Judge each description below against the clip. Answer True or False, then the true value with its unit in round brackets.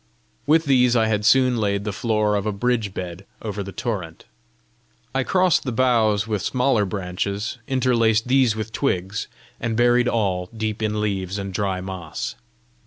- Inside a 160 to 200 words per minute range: True (165 wpm)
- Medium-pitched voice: False (110 Hz)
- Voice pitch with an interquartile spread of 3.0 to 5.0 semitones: True (3.6 semitones)